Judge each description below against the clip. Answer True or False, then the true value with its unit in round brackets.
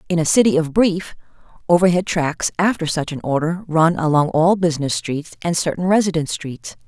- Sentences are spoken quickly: False (175 wpm)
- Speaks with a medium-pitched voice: True (165 Hz)